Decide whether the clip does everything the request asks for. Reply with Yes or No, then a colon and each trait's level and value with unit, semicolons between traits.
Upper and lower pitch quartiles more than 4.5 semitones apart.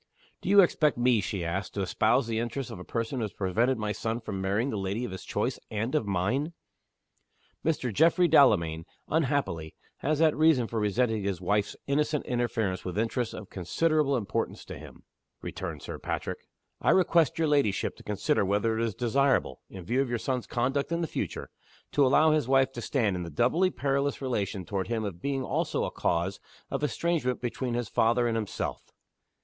Yes: wide, 5.5 semitones